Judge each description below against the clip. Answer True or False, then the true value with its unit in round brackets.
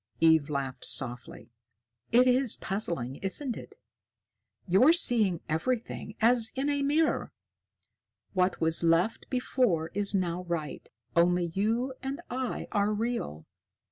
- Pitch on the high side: True (200 Hz)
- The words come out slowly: True (120 wpm)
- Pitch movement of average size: False (7.1 semitones)